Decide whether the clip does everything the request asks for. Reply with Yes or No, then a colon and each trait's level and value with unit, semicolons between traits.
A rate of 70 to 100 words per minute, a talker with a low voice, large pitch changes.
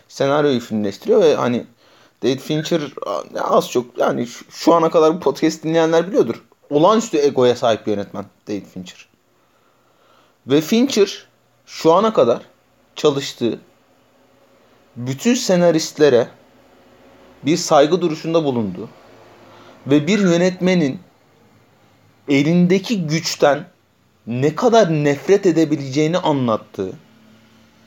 No: slow, 95 wpm; medium, 150 Hz; wide, 6.4 semitones